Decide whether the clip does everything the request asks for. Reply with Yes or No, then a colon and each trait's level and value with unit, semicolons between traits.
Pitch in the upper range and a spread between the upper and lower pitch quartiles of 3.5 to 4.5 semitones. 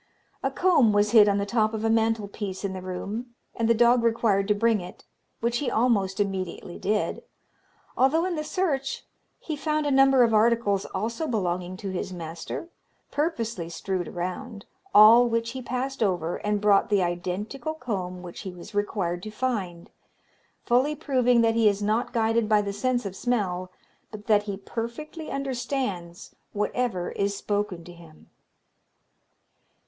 Yes: high, 215 Hz; average, 4.1 semitones